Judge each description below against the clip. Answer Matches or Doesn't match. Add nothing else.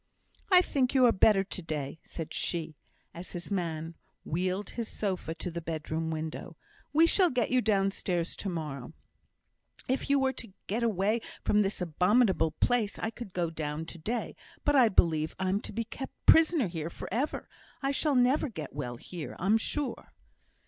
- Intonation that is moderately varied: Doesn't match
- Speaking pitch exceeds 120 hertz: Matches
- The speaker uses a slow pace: Doesn't match